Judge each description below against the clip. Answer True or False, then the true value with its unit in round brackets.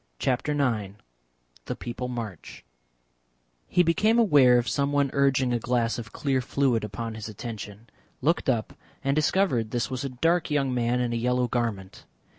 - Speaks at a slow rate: False (160 wpm)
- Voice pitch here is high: False (125 Hz)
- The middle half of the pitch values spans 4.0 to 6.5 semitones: False (3.2 semitones)